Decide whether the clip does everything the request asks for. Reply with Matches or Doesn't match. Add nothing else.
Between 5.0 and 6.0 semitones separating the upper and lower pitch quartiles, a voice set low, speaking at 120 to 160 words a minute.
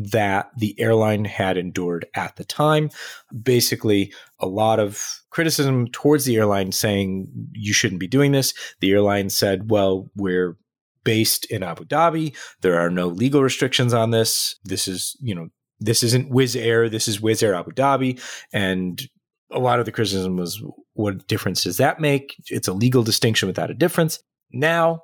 Doesn't match